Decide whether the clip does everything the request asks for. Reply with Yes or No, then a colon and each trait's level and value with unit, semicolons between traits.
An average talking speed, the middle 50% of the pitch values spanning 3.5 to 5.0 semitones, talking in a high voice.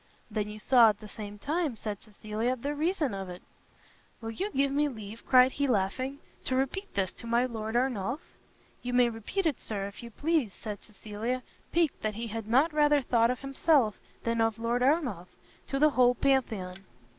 Yes: average, 190 wpm; average, 4.3 semitones; high, 235 Hz